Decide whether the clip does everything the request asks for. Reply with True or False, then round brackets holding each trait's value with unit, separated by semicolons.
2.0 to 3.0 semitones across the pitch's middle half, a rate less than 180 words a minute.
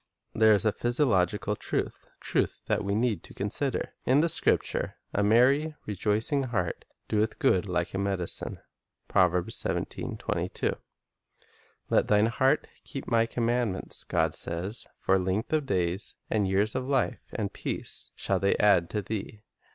False (4.1 semitones; 150 wpm)